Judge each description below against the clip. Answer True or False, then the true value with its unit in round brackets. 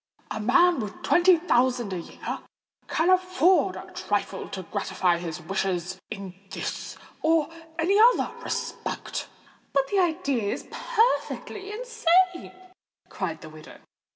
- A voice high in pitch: True (320 Hz)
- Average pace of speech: False (125 wpm)